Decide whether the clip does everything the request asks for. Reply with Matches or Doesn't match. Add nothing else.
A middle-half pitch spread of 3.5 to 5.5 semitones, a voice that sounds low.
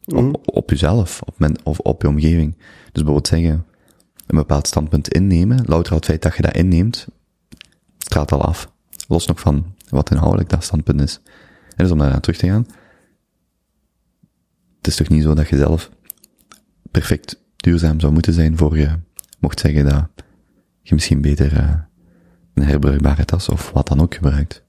Doesn't match